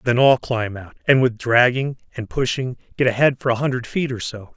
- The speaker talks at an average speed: No, fast, 225 wpm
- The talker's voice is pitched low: Yes, low, 125 Hz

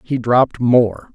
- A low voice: Yes, low, 120 Hz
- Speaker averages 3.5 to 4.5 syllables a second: Yes, 3.9 syllables/s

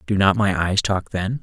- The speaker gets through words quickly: Yes, fast, 255 wpm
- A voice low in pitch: Yes, low, 100 Hz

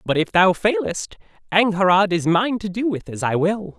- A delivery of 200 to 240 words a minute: Yes, fast, 205 wpm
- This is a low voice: No, high, 190 Hz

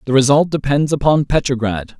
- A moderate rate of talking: Yes, average, 150 wpm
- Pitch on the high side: No, low, 135 Hz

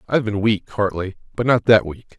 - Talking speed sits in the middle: No, fast, 220 wpm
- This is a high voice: No, low, 105 Hz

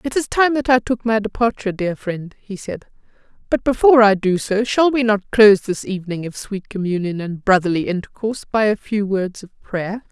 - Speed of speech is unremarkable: No, fast, 210 wpm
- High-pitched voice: Yes, high, 210 Hz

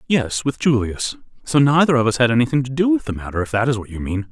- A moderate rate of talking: No, fast, 280 wpm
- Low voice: Yes, low, 120 Hz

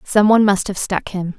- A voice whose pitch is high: Yes, high, 200 Hz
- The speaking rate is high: Yes, fast, 260 wpm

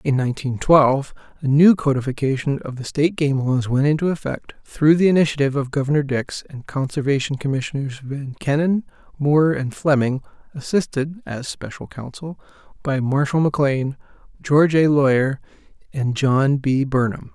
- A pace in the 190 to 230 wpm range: No, average, 145 wpm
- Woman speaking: No, male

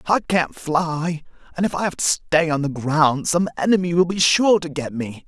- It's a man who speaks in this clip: Yes, male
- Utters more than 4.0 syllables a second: Yes, 4.8 syllables/s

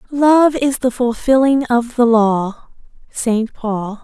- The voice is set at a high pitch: Yes, high, 245 Hz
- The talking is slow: Yes, slow, 120 wpm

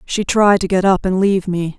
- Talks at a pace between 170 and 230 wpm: No, fast, 270 wpm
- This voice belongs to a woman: Yes, female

